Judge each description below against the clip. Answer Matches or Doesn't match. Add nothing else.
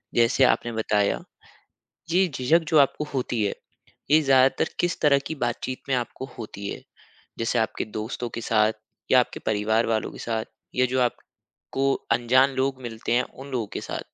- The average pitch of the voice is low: Matches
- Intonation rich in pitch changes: Doesn't match